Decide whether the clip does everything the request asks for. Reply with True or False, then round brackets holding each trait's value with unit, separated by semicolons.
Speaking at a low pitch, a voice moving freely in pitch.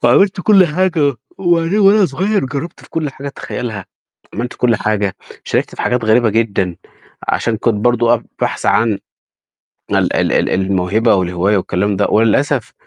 True (120 Hz; 6.9 semitones)